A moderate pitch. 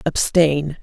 Yes: medium, 155 Hz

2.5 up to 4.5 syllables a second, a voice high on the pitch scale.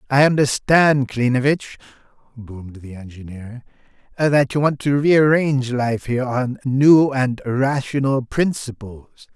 No: 4.3 syllables/s; low, 130 Hz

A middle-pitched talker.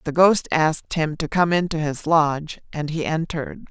Yes: medium, 160 Hz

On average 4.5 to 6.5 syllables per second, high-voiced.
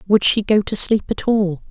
Yes: 4.6 syllables/s; high, 205 Hz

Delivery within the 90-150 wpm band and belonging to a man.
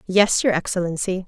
No: average, 140 wpm; female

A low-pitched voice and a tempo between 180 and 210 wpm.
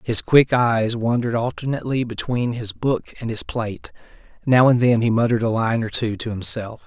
Yes: low, 115 Hz; average, 190 wpm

